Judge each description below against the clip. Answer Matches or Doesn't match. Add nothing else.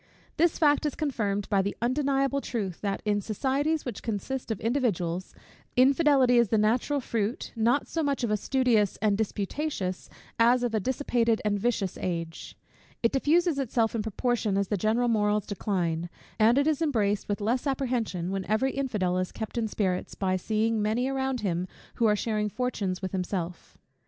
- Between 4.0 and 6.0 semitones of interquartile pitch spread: Matches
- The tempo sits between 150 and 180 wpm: Matches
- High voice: Matches